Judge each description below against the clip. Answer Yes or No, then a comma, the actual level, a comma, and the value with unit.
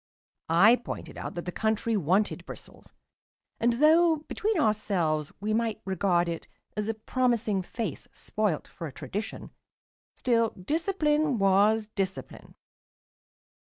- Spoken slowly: Yes, slow, 125 wpm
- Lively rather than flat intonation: No, average, 4.0 semitones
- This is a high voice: Yes, high, 215 Hz